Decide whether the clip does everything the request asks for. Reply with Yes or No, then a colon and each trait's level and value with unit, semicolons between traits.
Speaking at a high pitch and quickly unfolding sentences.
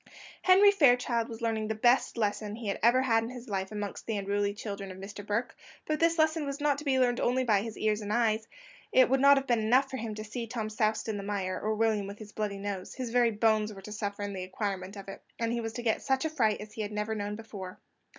Yes: high, 220 Hz; fast, 270 wpm